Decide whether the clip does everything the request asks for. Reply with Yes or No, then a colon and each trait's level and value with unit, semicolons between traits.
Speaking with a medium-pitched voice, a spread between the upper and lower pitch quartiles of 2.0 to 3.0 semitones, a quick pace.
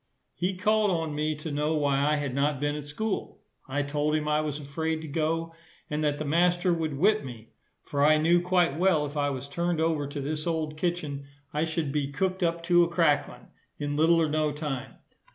Yes: medium, 155 Hz; narrow, 2.6 semitones; fast, 215 wpm